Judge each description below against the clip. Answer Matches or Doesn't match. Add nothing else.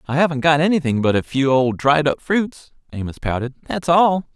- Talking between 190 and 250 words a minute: Matches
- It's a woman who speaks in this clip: Doesn't match